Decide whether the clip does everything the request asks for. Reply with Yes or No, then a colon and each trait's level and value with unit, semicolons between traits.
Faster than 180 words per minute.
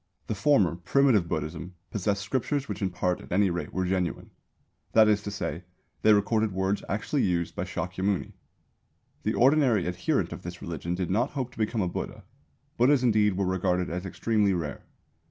No: average, 175 wpm